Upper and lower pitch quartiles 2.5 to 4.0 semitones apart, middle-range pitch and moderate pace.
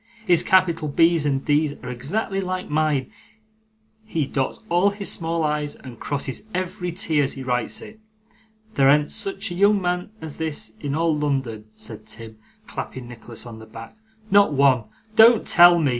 No: average, 5.2 semitones; medium, 150 Hz; average, 175 wpm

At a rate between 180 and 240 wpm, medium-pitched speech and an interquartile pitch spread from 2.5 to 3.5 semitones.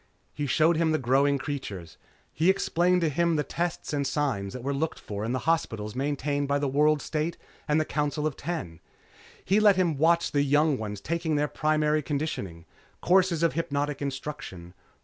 Yes: average, 185 wpm; medium, 150 Hz; average, 3.1 semitones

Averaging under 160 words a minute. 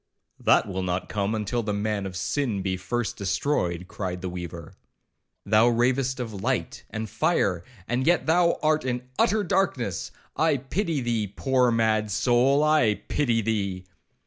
Yes: average, 150 wpm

